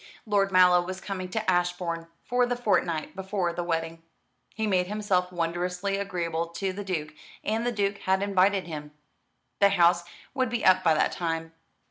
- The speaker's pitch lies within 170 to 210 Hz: Yes, medium, 185 Hz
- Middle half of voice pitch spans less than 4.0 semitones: Yes, average, 2.8 semitones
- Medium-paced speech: Yes, average, 175 wpm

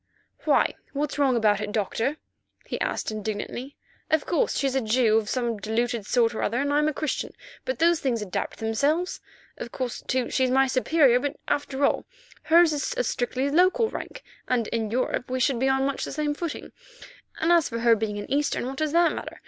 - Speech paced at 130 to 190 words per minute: No, average, 200 wpm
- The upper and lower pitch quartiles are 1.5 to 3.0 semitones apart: No, average, 4.3 semitones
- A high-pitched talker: Yes, very high, 260 Hz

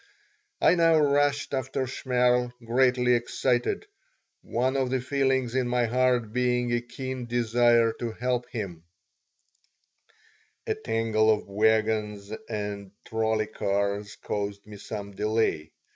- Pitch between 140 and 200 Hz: No, low, 120 Hz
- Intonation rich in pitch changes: No, average, 2.9 semitones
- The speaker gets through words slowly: Yes, slow, 120 wpm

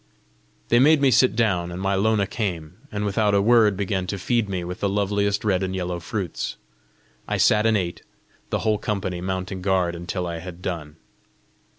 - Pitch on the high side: No, very low, 95 Hz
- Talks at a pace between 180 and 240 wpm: Yes, average, 190 wpm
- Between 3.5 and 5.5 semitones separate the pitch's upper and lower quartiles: No, average, 2.8 semitones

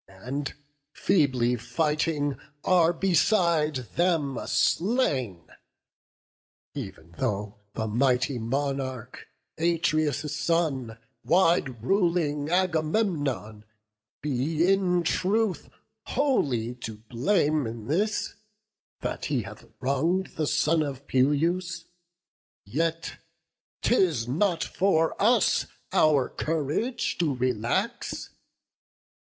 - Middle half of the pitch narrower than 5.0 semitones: No, average, 5.3 semitones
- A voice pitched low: No, medium, 150 Hz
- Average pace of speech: No, slow, 85 wpm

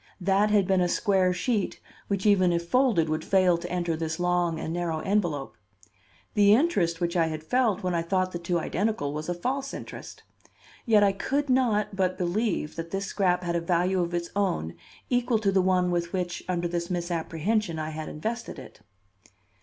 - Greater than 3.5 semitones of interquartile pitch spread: No, average, 3.1 semitones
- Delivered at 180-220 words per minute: Yes, average, 195 wpm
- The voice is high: No, medium, 180 Hz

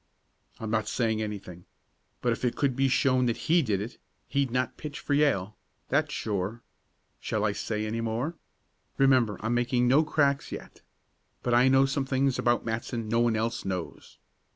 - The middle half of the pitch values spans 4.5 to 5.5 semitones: No, average, 3.6 semitones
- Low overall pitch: Yes, low, 120 Hz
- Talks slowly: No, average, 175 wpm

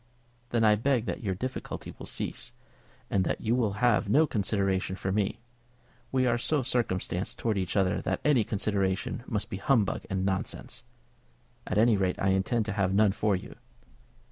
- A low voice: Yes, low, 105 Hz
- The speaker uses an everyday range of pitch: Yes, average, 3.6 semitones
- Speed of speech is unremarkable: Yes, average, 175 wpm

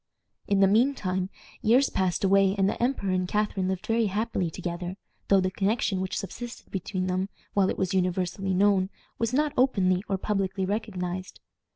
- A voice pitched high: Yes, high, 195 Hz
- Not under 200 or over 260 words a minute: No, average, 175 wpm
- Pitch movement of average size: No, narrow, 2.3 semitones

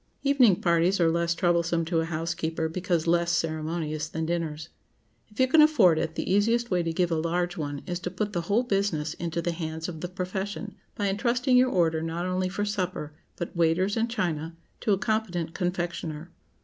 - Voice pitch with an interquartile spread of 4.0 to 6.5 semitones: No, average, 3.3 semitones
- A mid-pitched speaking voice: Yes, medium, 175 Hz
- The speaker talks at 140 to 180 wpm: No, average, 195 wpm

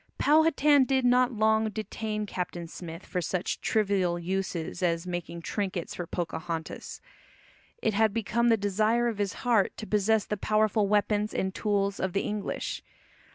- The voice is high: Yes, high, 205 Hz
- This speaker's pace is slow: No, average, 155 wpm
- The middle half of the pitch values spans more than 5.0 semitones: No, average, 3.2 semitones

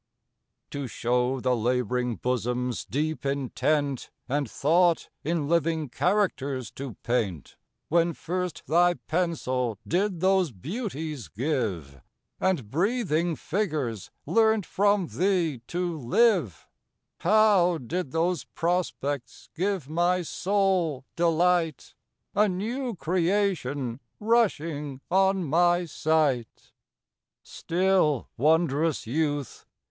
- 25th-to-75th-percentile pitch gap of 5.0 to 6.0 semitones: Yes, wide, 5.6 semitones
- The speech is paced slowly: Yes, slow, 95 wpm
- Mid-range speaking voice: Yes, medium, 160 Hz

